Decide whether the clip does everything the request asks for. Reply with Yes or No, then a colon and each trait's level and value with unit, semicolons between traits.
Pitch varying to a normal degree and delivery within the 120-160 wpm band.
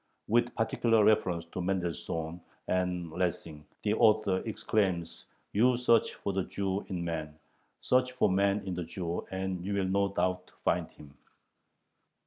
Yes: average, 3.3 semitones; average, 145 wpm